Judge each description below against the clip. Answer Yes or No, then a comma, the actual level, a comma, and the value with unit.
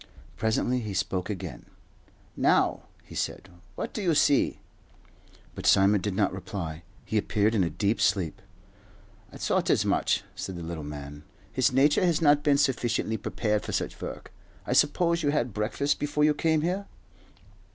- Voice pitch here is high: No, low, 110 Hz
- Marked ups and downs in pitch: Yes, wide, 7.5 semitones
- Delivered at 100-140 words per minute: No, average, 165 wpm